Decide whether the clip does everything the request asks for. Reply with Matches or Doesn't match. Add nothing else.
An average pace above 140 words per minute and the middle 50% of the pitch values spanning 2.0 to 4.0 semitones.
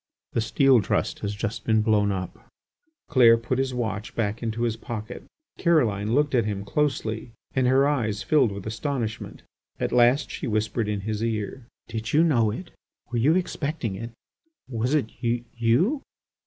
Matches